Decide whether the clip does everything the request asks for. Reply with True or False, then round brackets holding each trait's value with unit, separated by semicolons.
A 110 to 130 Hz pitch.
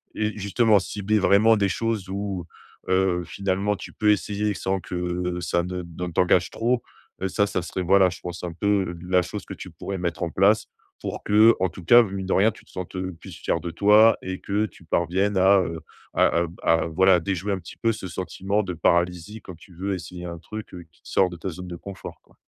False (95 Hz)